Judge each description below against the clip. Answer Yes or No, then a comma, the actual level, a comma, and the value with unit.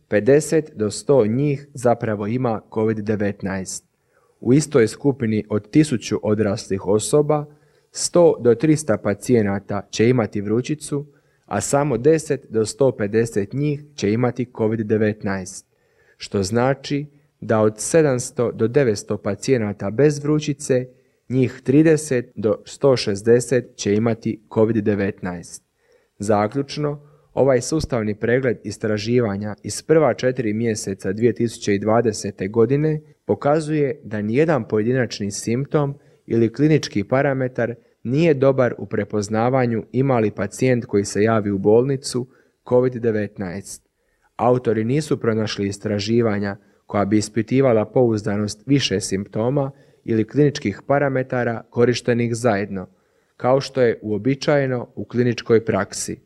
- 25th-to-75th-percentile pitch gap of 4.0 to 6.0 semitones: Yes, average, 4.5 semitones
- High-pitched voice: No, low, 115 Hz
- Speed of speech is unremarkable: No, slow, 105 wpm